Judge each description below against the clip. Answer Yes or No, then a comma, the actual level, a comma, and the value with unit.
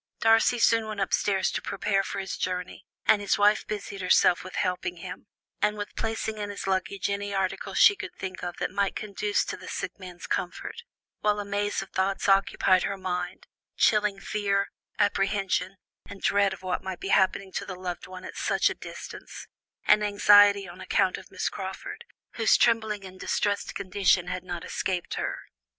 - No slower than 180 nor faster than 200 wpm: Yes, average, 185 wpm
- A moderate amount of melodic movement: No, narrow, 1.8 semitones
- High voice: Yes, high, 195 Hz